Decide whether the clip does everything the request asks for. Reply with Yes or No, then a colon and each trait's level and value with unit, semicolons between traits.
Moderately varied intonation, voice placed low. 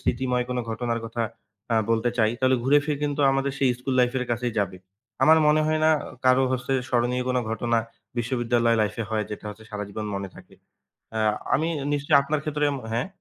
Yes: average, 3.1 semitones; low, 125 Hz